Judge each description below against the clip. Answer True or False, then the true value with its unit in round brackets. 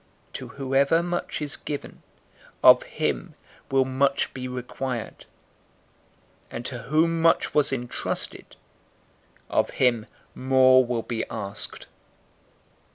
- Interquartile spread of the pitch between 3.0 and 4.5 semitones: False (2.4 semitones)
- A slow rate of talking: True (105 wpm)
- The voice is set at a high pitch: False (130 Hz)